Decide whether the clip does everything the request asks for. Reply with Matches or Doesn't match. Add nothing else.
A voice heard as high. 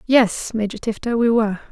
Matches